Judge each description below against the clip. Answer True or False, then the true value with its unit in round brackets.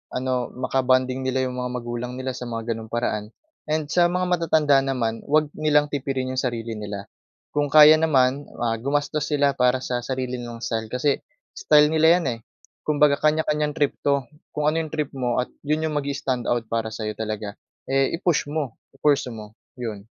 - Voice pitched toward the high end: False (130 Hz)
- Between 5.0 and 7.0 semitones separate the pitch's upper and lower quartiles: False (3.7 semitones)